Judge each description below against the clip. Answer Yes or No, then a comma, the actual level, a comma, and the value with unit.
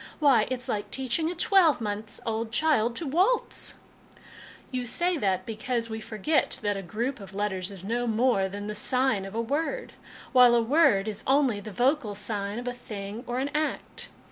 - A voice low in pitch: No, high, 230 Hz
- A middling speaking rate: Yes, average, 195 wpm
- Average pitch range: Yes, average, 4.5 semitones